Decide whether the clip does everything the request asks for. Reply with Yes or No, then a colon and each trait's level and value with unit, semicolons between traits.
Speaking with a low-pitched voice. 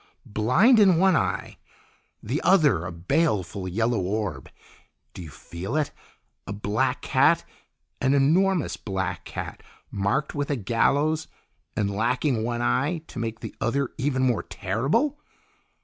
Yes: low, 125 Hz